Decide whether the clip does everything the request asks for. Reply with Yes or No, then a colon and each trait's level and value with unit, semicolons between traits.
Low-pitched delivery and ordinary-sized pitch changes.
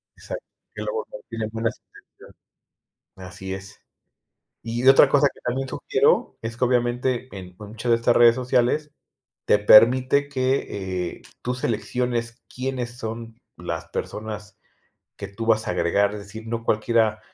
Yes: low, 115 Hz; average, 3.1 semitones